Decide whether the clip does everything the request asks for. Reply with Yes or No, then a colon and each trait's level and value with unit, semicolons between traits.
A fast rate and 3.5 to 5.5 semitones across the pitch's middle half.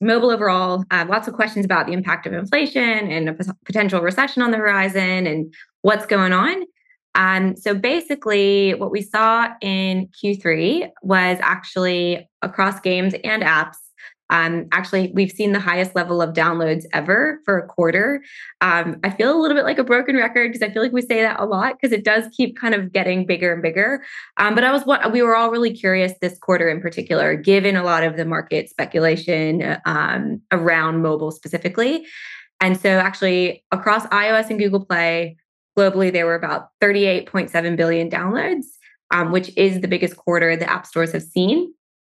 No: average, 185 wpm; average, 4.1 semitones